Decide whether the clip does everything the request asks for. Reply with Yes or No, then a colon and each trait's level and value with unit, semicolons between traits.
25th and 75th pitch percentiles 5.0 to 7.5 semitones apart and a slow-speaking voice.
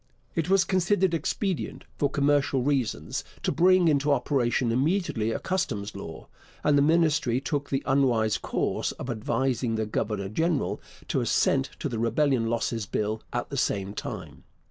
No: wide, 5.5 semitones; average, 155 wpm